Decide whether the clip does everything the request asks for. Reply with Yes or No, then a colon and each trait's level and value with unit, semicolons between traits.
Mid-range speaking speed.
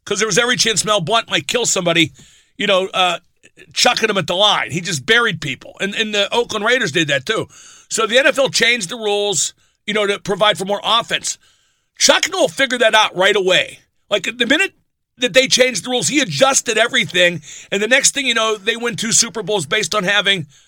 No: fast, 220 wpm